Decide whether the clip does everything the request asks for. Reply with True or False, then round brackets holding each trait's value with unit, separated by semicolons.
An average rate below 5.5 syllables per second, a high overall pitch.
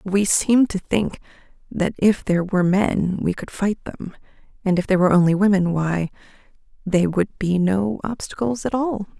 True (5.0 syllables/s; 195 Hz)